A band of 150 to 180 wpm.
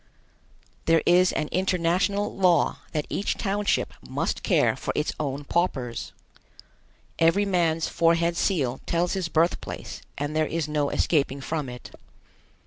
No: slow, 135 wpm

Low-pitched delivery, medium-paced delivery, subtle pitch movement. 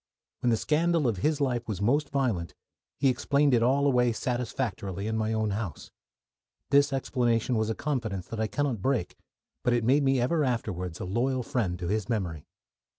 No: low, 120 Hz; average, 185 wpm; average, 4.1 semitones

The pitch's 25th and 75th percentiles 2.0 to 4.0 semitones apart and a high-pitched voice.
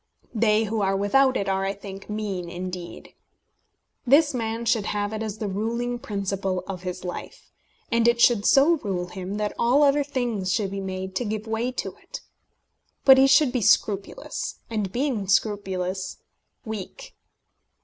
Yes: average, 3.6 semitones; high, 210 Hz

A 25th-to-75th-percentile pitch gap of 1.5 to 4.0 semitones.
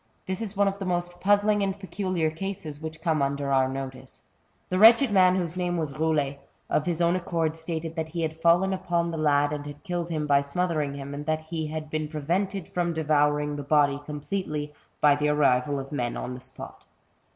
Yes: average, 3.4 semitones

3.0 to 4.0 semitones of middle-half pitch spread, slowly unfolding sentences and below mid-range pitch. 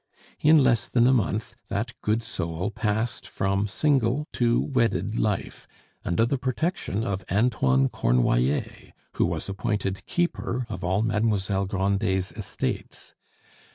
Yes: average, 3.7 semitones; slow, 125 wpm; low, 105 Hz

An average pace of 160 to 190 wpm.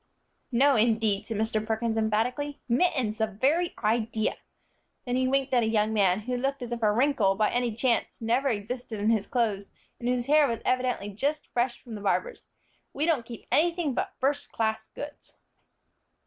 Yes: average, 180 wpm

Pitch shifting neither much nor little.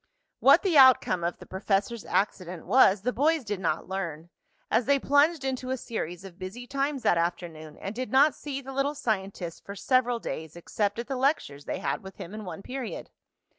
No: wide, 6.7 semitones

